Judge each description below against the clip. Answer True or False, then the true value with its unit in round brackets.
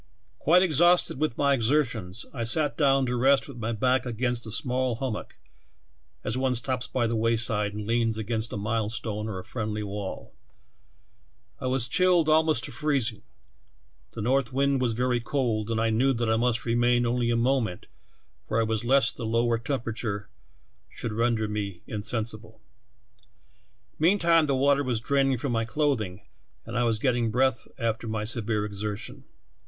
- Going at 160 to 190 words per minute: True (170 wpm)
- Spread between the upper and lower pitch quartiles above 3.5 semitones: False (3.2 semitones)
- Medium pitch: False (120 Hz)